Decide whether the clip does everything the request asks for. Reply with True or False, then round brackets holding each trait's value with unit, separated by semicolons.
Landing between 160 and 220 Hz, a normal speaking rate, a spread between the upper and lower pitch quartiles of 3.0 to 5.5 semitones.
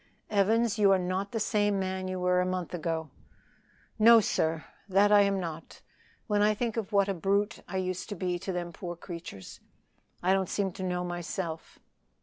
False (190 Hz; 190 wpm; 2.5 semitones)